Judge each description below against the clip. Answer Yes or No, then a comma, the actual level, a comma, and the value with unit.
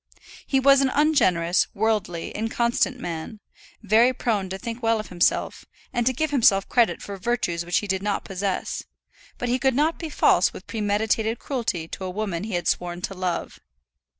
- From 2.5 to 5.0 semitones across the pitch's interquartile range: Yes, average, 4.6 semitones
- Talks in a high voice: Yes, high, 215 Hz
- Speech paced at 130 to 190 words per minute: Yes, average, 180 wpm